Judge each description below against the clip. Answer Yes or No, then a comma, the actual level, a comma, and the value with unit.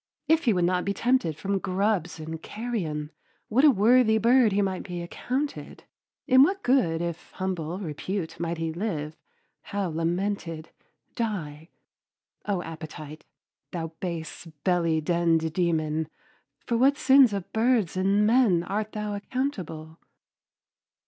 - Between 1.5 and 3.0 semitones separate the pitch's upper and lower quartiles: No, average, 5.2 semitones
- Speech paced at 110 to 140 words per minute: Yes, slow, 135 wpm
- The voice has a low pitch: No, medium, 185 Hz